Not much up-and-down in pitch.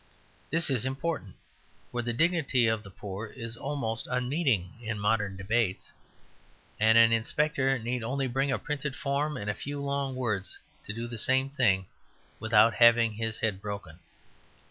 No: average, 4.0 semitones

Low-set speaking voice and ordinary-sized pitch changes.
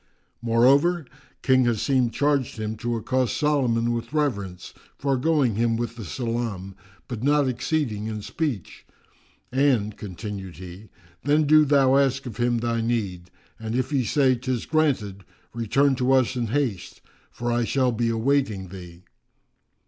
Yes: low, 120 Hz; average, 3.9 semitones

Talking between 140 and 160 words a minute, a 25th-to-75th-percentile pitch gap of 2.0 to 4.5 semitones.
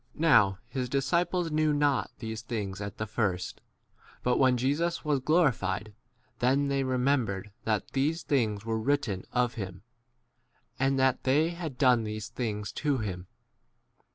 No: average, 155 wpm; average, 5.0 semitones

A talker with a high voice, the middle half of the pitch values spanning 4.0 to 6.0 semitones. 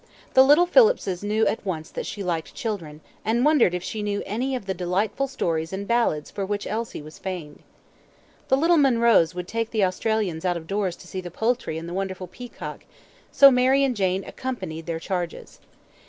Yes: high, 200 Hz; average, 5.2 semitones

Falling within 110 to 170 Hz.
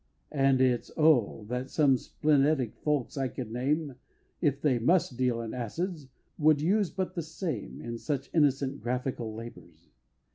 Yes: low, 135 Hz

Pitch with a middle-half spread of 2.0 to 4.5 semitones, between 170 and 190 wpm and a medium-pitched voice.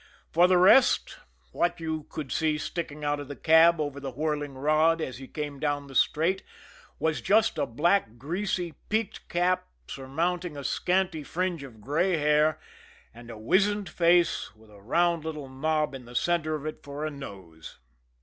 Yes: average, 3.7 semitones; average, 175 wpm; medium, 155 Hz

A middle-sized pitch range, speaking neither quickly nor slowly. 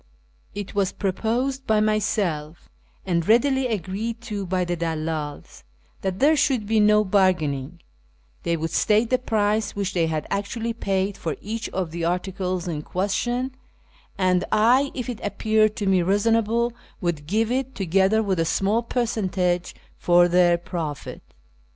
Yes: average, 4.1 semitones; average, 150 wpm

